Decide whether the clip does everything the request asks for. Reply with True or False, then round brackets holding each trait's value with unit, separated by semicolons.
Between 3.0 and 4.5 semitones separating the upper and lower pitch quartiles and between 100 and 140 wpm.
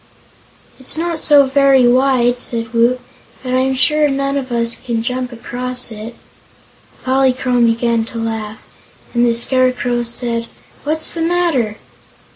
False (2.4 semitones; 135 wpm)